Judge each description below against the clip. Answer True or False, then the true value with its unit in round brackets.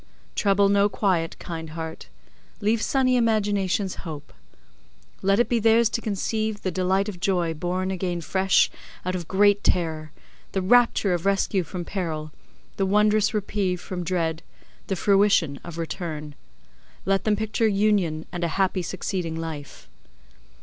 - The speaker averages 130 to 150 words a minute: True (145 wpm)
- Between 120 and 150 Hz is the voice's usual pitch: False (190 Hz)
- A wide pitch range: False (3.4 semitones)